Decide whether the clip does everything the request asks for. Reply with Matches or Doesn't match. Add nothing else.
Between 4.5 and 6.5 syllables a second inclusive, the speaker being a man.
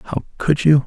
Doesn't match